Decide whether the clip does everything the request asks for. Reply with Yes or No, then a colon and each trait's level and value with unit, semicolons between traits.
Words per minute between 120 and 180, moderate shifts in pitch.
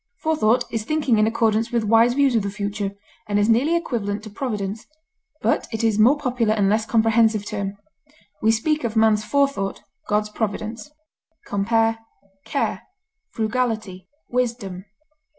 No: average, 150 wpm; narrow, 2.3 semitones